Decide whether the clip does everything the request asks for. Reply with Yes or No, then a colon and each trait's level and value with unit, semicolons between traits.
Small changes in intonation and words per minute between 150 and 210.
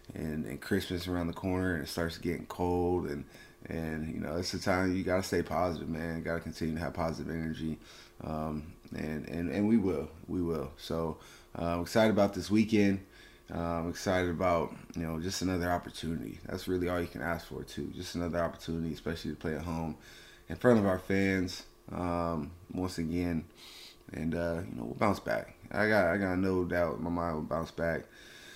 Yes: narrow, 2.2 semitones; fast, 205 wpm